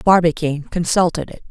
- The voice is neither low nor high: Yes, medium, 170 Hz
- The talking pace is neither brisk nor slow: No, slow, 120 wpm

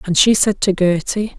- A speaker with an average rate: No, fast, 215 wpm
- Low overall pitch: No, high, 195 Hz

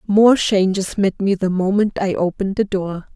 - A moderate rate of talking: Yes, average, 190 wpm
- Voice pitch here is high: Yes, high, 195 Hz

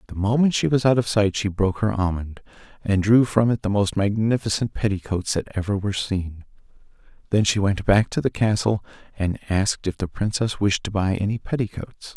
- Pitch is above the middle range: No, low, 100 Hz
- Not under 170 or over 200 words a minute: Yes, average, 195 wpm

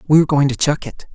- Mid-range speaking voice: Yes, medium, 145 Hz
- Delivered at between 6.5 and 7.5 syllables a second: No, 6.0 syllables/s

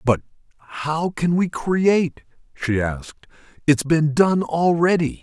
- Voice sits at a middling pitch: Yes, medium, 155 Hz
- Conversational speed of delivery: No, slow, 115 wpm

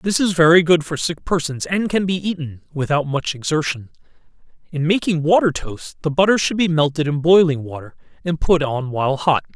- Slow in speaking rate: No, average, 195 wpm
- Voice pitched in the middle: Yes, medium, 155 Hz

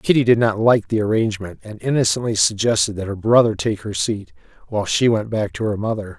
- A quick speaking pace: Yes, fast, 215 wpm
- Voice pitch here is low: Yes, low, 110 Hz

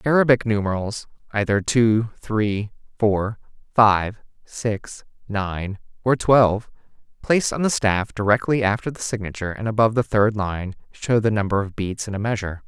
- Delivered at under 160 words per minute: Yes, average, 150 wpm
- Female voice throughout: No, male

